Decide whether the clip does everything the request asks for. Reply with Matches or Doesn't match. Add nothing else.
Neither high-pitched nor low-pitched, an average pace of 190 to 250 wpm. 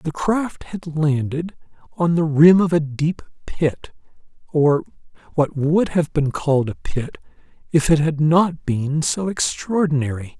Doesn't match